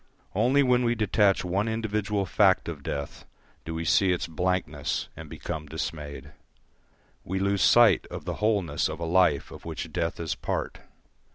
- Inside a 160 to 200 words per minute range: Yes, average, 165 wpm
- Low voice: Yes, very low, 90 Hz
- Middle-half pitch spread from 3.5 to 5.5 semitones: Yes, average, 4.6 semitones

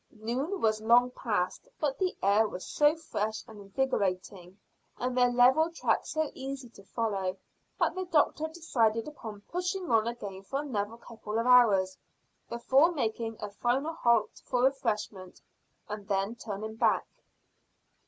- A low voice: No, high, 230 Hz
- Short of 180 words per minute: Yes, average, 145 wpm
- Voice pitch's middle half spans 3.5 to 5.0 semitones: Yes, average, 4.6 semitones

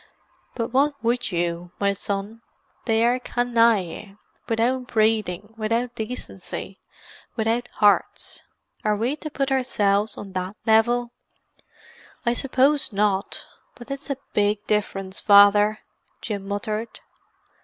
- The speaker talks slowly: Yes, slow, 110 wpm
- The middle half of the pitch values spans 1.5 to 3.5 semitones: Yes, average, 3.1 semitones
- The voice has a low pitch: No, high, 220 Hz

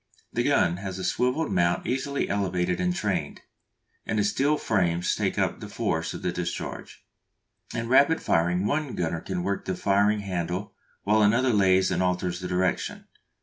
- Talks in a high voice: No, very low, 95 Hz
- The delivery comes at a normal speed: Yes, average, 170 wpm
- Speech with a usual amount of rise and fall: Yes, average, 3.4 semitones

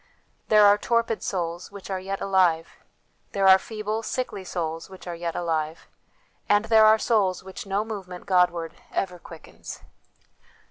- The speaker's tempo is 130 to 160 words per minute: Yes, average, 150 wpm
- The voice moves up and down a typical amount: Yes, average, 3.2 semitones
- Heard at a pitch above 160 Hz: Yes, high, 190 Hz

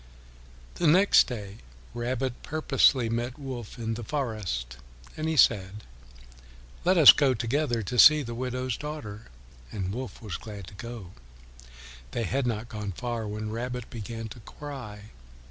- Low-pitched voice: Yes, low, 120 Hz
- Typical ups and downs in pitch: Yes, average, 3.6 semitones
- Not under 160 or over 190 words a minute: No, average, 145 wpm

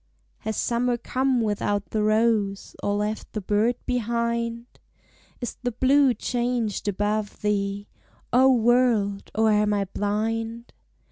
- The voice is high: Yes, high, 225 Hz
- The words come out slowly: Yes, slow, 125 wpm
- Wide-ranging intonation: No, narrow, 2.6 semitones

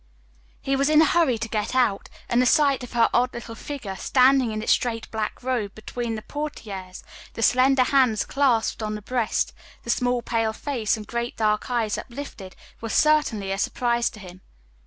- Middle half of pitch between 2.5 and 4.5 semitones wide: Yes, average, 3.2 semitones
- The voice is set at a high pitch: Yes, high, 235 Hz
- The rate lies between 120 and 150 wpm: No, average, 190 wpm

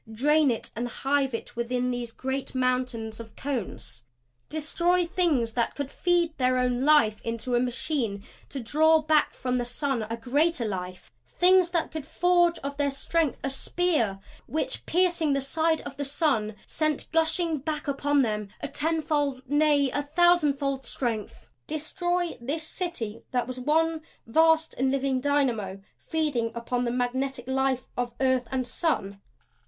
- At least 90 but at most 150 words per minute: No, average, 160 wpm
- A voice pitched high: Yes, very high, 275 Hz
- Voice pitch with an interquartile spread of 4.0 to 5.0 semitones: Yes, average, 4.3 semitones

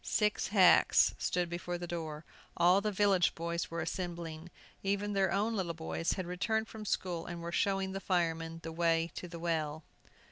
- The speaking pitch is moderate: Yes, medium, 175 Hz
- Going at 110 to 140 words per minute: No, average, 180 wpm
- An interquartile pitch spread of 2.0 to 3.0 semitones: Yes, average, 2.7 semitones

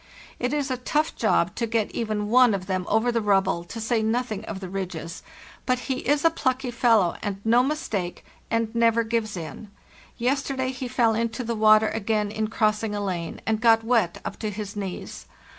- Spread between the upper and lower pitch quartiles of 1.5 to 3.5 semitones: Yes, average, 2.9 semitones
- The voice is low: No, high, 225 Hz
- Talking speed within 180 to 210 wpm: Yes, average, 195 wpm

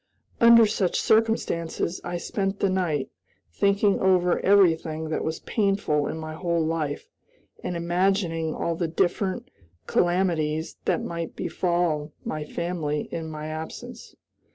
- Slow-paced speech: Yes, slow, 130 wpm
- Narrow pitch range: No, average, 3.3 semitones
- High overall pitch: No, medium, 170 Hz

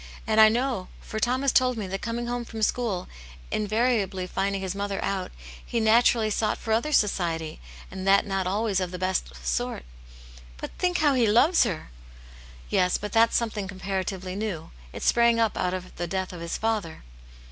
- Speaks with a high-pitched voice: Yes, high, 200 Hz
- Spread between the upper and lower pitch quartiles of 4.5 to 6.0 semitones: No, average, 3.8 semitones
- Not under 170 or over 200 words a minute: Yes, average, 195 wpm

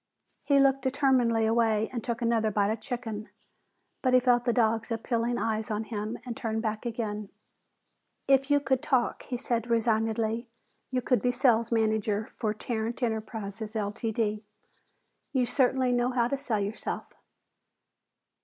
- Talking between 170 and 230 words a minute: No, average, 150 wpm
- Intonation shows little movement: Yes, narrow, 2.2 semitones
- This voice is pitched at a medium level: No, high, 230 Hz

